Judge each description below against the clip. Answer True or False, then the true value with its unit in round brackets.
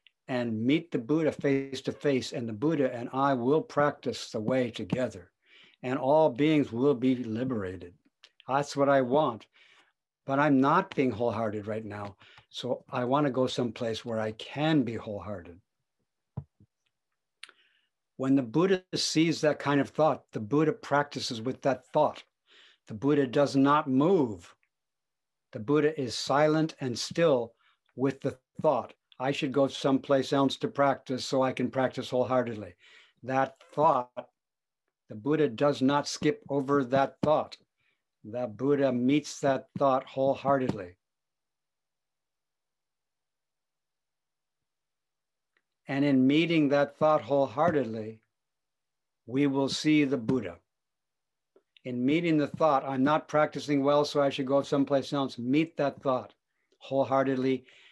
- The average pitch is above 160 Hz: False (135 Hz)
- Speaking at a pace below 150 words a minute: True (135 wpm)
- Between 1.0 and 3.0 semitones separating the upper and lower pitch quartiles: True (2.4 semitones)